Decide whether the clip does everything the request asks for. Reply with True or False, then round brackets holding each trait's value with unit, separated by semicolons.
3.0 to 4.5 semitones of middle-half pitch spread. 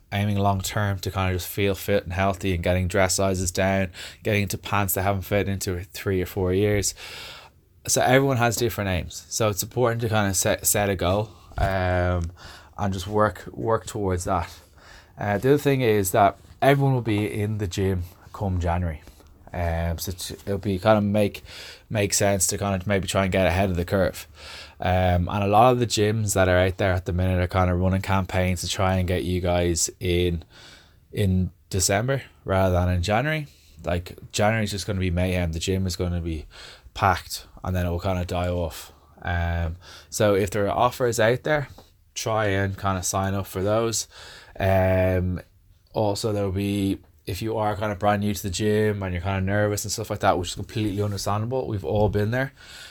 False (2.4 semitones)